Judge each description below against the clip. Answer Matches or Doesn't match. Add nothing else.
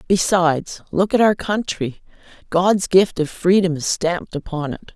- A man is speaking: Doesn't match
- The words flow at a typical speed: Matches